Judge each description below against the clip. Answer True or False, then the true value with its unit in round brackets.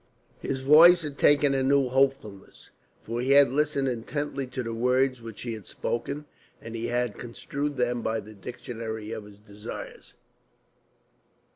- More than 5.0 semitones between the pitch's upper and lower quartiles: False (3.4 semitones)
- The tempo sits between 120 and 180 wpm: True (155 wpm)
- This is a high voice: False (125 Hz)